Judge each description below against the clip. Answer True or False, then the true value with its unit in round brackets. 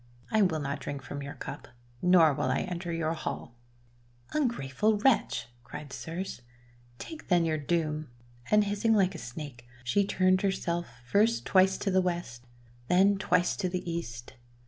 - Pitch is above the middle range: False (170 Hz)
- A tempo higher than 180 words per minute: False (170 wpm)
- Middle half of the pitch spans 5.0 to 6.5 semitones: True (5.5 semitones)